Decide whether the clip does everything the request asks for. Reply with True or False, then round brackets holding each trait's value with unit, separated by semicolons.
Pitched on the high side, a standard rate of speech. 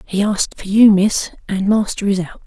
False (200 Hz; 220 wpm)